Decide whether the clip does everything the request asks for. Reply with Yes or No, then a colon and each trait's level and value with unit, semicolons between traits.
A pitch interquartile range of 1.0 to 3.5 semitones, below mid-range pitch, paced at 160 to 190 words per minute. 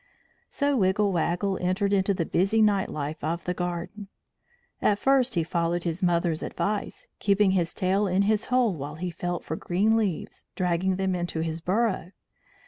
No: average, 3.0 semitones; medium, 185 Hz; average, 170 wpm